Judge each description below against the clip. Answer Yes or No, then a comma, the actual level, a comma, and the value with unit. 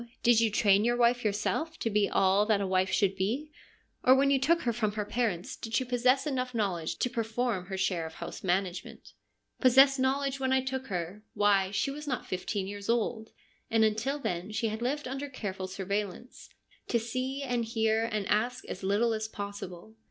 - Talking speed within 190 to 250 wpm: Yes, fast, 205 wpm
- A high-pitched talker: Yes, high, 220 Hz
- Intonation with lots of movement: No, average, 4.2 semitones